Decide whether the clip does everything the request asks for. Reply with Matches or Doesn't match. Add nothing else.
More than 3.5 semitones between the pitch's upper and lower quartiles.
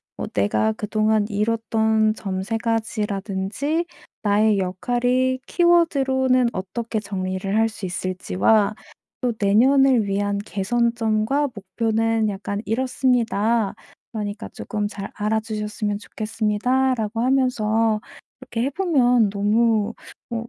Doesn't match